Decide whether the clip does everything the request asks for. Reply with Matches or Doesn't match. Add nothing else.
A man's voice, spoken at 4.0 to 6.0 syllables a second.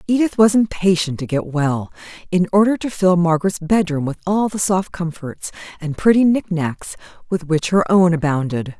Doesn't match